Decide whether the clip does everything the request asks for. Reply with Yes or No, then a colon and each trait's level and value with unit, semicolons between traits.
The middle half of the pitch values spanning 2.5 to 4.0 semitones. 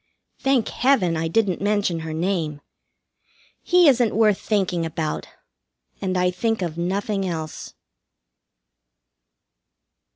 No: average, 4.6 semitones